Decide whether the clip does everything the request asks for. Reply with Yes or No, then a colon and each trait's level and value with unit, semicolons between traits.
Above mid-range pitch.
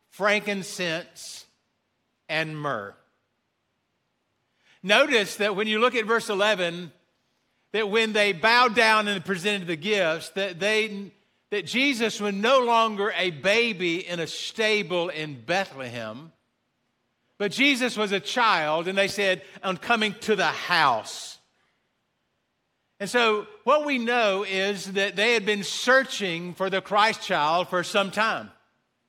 Yes: high, 200 Hz